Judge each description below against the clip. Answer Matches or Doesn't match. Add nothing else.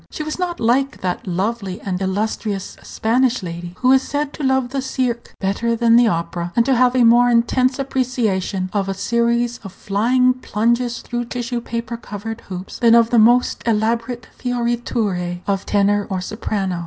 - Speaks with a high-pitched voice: Matches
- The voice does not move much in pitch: Doesn't match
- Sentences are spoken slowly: Doesn't match